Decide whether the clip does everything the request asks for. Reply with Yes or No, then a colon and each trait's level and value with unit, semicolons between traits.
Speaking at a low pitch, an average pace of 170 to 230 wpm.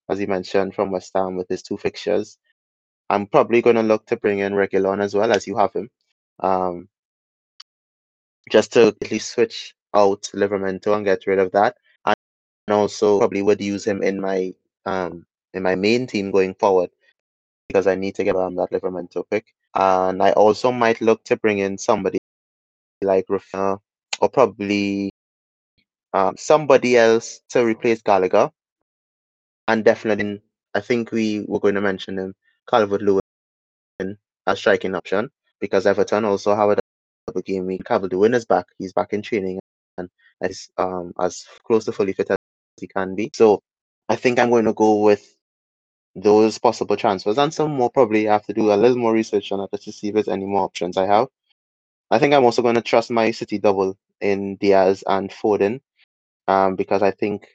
Yes: low, 100 Hz; average, 180 wpm